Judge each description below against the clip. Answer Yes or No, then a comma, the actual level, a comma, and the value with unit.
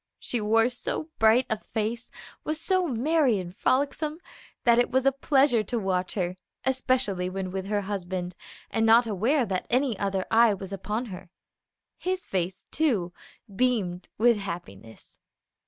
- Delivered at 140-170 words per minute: Yes, average, 155 wpm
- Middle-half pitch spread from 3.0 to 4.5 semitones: No, average, 5.2 semitones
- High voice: Yes, high, 220 Hz